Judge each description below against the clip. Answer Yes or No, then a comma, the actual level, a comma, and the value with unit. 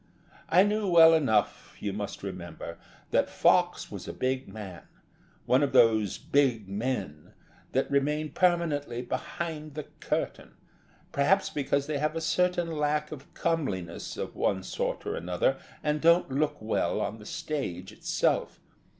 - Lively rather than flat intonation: Yes, wide, 6.6 semitones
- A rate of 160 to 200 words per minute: No, average, 145 wpm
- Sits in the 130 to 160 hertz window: Yes, medium, 140 Hz